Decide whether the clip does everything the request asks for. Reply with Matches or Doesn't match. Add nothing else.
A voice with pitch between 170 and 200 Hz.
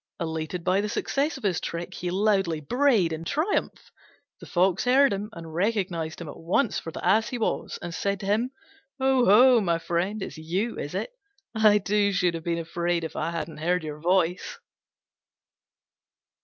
Matches